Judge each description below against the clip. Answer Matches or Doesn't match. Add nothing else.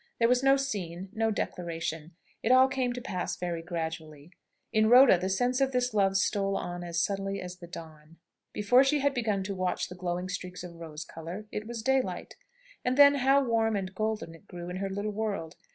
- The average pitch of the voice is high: Matches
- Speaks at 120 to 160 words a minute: Doesn't match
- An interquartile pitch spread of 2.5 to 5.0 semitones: Doesn't match